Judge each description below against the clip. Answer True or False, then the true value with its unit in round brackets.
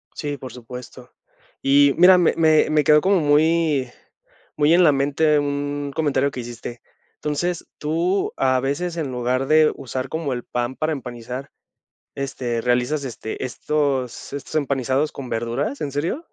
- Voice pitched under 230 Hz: True (140 Hz)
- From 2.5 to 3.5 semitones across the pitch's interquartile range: True (3.2 semitones)